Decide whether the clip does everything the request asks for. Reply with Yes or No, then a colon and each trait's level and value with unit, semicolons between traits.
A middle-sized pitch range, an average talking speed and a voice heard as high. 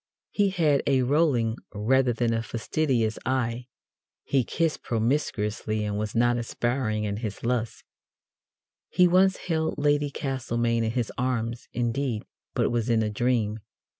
No: average, 3.6 semitones; average, 145 wpm; low, 120 Hz